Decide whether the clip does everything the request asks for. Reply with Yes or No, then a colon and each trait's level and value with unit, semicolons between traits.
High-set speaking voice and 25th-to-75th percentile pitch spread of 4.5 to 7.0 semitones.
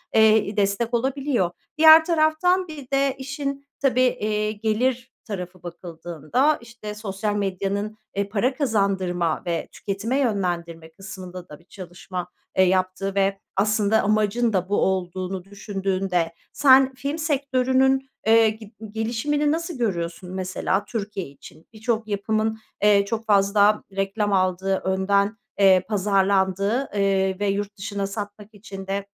No: high, 205 Hz; average, 3.7 semitones